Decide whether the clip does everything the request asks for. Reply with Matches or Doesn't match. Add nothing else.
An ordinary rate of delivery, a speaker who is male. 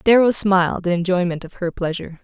Doesn't match